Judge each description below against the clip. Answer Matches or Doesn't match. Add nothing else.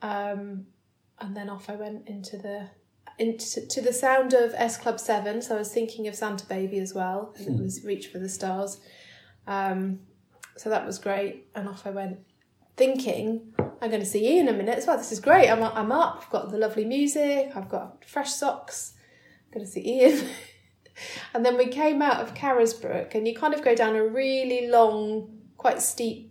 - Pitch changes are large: Doesn't match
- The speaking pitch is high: Matches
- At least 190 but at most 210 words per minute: Matches